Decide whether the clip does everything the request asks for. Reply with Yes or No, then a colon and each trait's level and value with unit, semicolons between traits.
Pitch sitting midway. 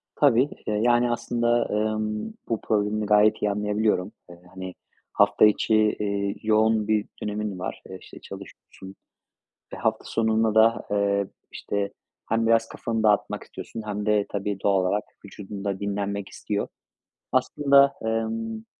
No: low, 105 Hz